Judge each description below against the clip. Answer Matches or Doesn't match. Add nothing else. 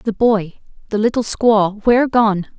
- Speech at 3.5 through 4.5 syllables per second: Matches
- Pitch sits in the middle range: Doesn't match